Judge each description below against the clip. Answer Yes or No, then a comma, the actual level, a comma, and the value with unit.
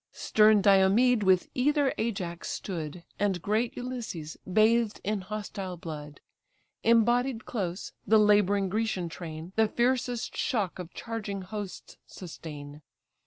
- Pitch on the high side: Yes, high, 205 Hz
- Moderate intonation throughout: Yes, average, 4.0 semitones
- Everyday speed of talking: No, slow, 120 wpm